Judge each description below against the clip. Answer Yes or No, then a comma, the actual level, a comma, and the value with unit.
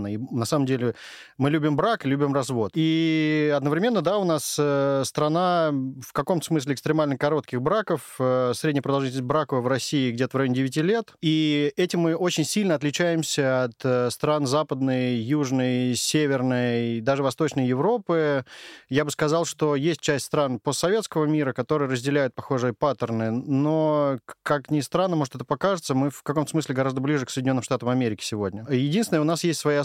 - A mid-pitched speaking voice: Yes, medium, 145 Hz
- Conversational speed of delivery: No, fast, 165 wpm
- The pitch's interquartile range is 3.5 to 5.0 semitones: No, average, 3.1 semitones